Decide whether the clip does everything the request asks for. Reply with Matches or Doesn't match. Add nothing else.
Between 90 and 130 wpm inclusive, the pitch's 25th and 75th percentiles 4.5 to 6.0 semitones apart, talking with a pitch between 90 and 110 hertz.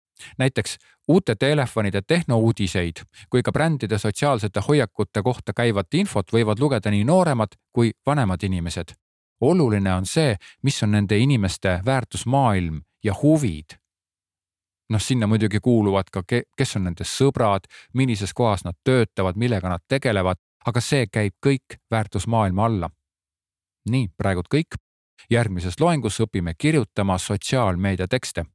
Matches